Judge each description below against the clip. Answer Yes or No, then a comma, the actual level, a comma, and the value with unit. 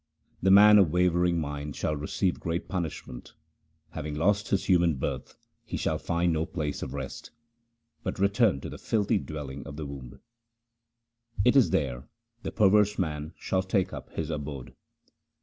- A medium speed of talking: Yes, average, 160 wpm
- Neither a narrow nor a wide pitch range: Yes, average, 4.6 semitones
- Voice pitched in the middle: No, very low, 85 Hz